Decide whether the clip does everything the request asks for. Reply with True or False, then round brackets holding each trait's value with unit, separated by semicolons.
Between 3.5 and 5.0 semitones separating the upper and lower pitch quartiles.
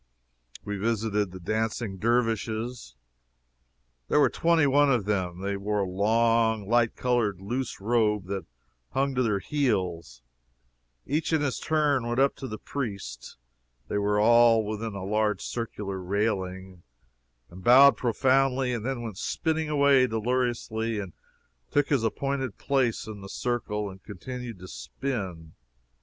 True (4.2 semitones)